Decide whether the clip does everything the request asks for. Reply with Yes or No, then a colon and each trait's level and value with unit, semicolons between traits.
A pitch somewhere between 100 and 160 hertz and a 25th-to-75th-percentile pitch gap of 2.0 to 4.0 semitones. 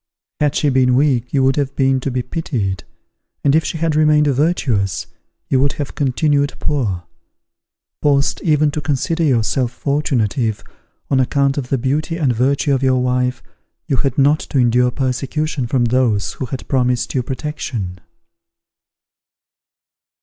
Yes: low, 135 Hz; average, 2.8 semitones